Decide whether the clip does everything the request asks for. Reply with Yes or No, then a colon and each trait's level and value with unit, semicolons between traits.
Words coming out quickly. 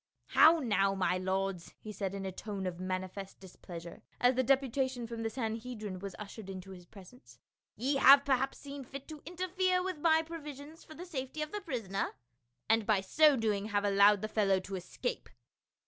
No: average, 195 wpm